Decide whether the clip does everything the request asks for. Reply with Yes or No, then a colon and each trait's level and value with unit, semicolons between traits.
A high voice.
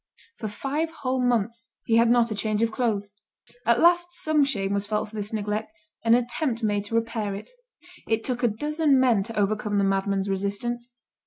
Yes: high, 225 Hz